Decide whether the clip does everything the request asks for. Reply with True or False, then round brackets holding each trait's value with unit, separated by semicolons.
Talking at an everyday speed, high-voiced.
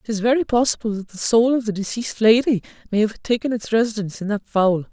False (220 wpm; 220 Hz)